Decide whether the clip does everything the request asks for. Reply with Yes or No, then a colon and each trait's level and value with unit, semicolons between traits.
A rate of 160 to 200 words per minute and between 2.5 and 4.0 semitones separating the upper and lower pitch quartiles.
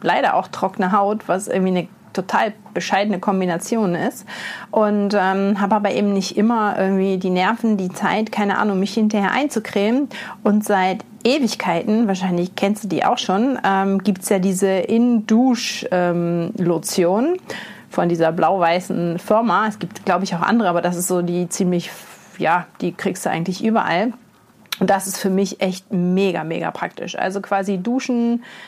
Yes: average, 165 wpm; average, 3.0 semitones